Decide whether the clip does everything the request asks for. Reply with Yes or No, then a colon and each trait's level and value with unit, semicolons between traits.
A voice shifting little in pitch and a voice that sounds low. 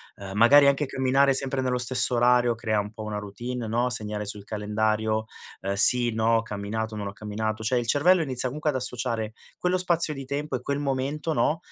No: average, 4.0 semitones; low, 120 Hz